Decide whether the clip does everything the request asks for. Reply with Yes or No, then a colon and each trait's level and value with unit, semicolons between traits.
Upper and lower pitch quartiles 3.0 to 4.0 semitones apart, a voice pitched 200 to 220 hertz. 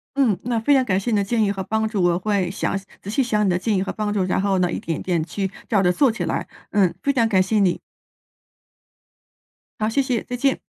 Yes: average, 3.5 semitones; high, 205 Hz